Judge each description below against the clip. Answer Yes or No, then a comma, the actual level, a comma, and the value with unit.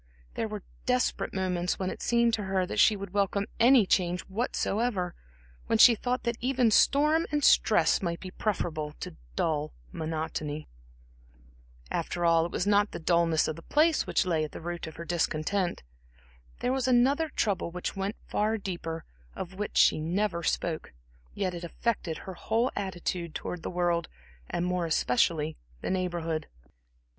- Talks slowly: No, average, 165 wpm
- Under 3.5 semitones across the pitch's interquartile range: No, average, 4.4 semitones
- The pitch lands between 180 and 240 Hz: Yes, medium, 185 Hz